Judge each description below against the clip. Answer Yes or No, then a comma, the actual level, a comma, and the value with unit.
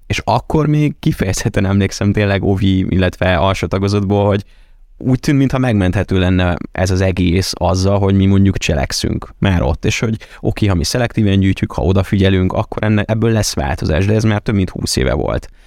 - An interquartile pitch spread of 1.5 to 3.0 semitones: Yes, average, 2.7 semitones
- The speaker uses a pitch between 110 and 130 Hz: No, low, 100 Hz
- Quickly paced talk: Yes, fast, 180 wpm